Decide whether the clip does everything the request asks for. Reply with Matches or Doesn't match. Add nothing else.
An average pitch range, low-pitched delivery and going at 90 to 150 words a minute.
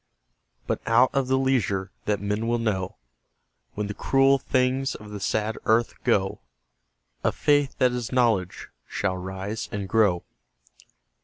Matches